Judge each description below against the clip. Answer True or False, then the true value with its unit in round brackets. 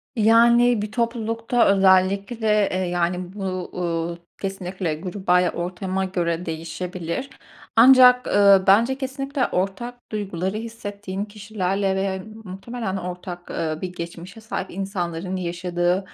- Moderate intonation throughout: True (3.6 semitones)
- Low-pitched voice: False (190 Hz)